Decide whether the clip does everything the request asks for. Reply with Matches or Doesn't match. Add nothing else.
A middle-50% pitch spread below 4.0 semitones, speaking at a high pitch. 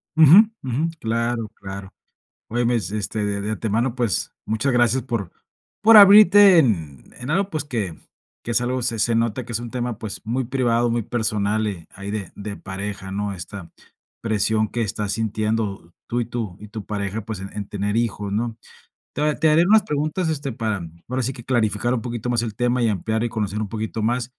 Doesn't match